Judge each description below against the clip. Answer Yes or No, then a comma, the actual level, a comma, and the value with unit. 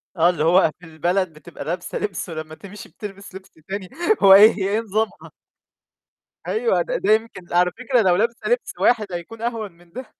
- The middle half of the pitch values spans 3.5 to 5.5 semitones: Yes, average, 4.1 semitones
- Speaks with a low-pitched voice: No, high, 195 Hz